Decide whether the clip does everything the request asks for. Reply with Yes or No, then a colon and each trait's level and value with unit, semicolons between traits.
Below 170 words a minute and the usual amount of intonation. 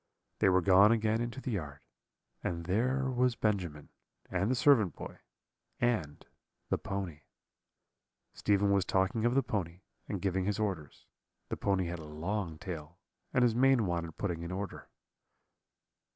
Yes: average, 150 wpm; average, 4.6 semitones